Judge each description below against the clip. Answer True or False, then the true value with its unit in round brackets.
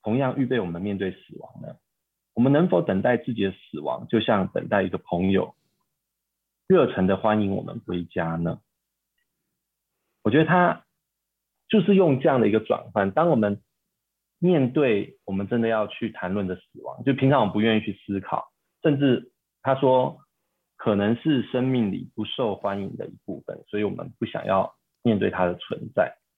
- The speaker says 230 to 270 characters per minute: True (255 characters per minute)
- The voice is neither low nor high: False (110 Hz)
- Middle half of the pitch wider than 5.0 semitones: True (5.6 semitones)